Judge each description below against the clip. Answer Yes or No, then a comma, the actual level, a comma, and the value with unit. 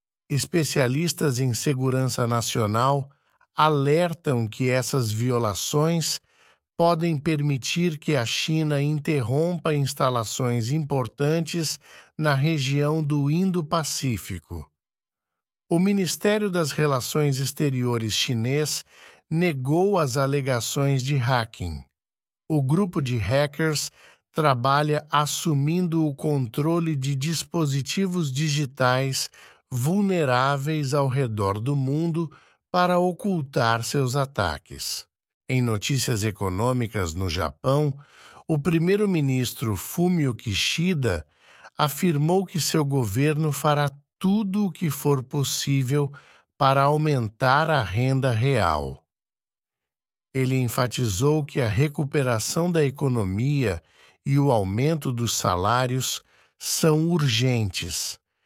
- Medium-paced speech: No, slow, 90 wpm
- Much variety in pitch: No, average, 3.9 semitones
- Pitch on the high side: No, medium, 140 Hz